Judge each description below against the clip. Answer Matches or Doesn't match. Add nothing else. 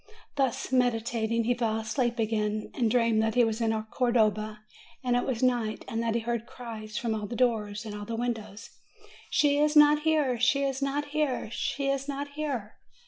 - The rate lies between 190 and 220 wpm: Matches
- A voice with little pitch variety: Doesn't match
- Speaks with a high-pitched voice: Matches